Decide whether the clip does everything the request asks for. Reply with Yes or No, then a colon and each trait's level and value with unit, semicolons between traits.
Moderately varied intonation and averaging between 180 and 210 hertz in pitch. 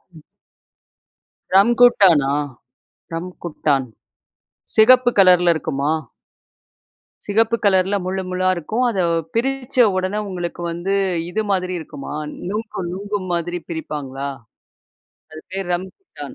Yes: average, 3.8 semitones; medium, 185 Hz